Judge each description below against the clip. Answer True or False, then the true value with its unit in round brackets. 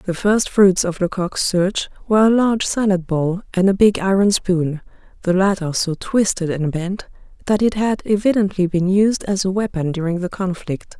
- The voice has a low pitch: False (190 Hz)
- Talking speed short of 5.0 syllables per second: True (4.8 syllables/s)